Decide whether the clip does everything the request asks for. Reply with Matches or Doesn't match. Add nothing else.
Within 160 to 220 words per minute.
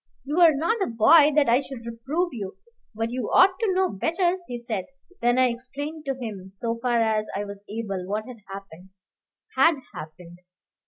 Matches